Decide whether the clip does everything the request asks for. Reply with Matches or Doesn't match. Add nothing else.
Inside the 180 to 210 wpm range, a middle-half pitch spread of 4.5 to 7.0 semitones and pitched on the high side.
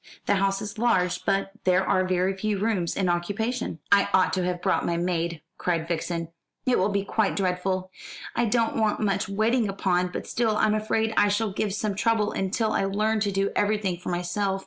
Doesn't match